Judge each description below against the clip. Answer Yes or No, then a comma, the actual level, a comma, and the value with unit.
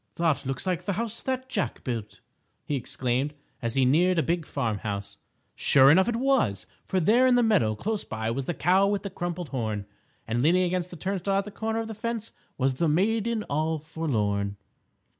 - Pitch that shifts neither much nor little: No, wide, 8.0 semitones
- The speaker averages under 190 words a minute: No, average, 200 wpm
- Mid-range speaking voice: Yes, medium, 170 Hz